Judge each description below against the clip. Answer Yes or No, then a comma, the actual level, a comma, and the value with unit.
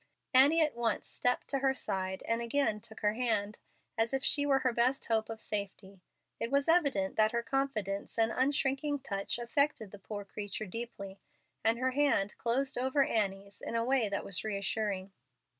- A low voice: No, high, 230 Hz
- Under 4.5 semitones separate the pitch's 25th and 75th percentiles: No, average, 4.8 semitones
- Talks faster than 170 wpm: Yes, average, 180 wpm